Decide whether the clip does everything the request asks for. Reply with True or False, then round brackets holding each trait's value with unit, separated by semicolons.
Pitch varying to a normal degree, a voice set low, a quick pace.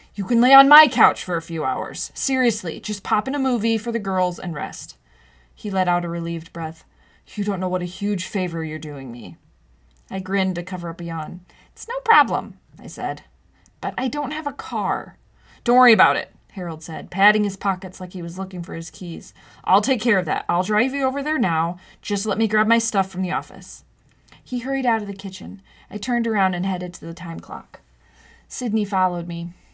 False (4.7 semitones; 190 Hz; 220 wpm)